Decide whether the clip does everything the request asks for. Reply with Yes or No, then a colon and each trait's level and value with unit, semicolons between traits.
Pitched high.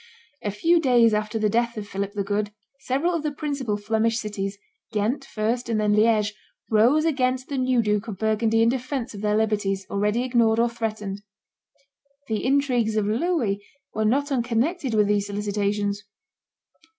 Yes: high, 220 Hz